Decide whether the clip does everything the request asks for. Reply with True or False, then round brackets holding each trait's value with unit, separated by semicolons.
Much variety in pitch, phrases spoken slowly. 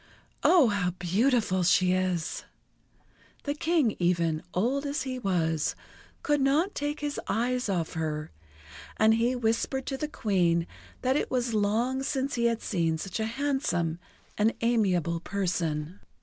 False (7.0 semitones; 145 wpm)